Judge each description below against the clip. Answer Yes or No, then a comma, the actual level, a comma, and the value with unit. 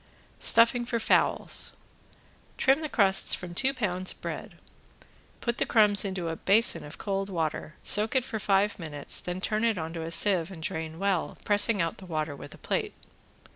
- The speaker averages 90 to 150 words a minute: No, average, 185 wpm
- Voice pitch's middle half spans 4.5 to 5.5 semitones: Yes, average, 4.8 semitones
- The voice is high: Yes, high, 195 Hz